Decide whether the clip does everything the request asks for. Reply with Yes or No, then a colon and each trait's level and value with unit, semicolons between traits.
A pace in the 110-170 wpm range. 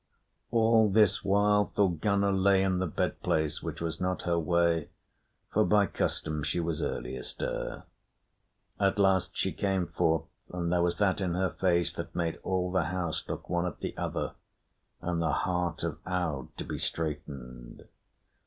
Yes: average, 165 wpm